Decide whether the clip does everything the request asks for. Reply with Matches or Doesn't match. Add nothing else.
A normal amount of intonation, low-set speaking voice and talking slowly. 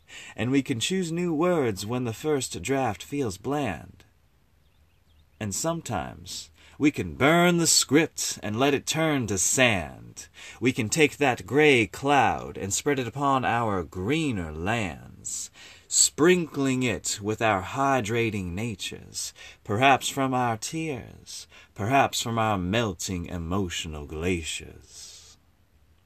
Doesn't match